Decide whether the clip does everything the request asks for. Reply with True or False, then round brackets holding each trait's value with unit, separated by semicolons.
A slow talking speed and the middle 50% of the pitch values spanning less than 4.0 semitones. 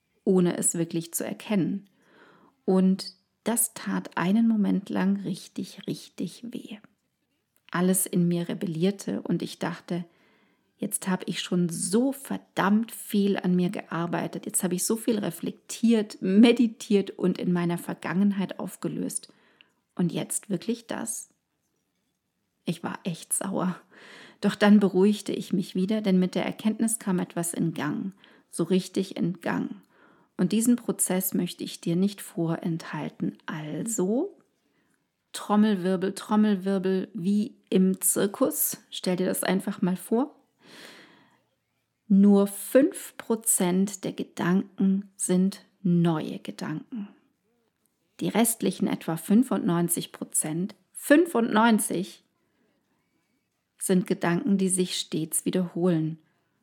True (115 wpm; 3.1 semitones)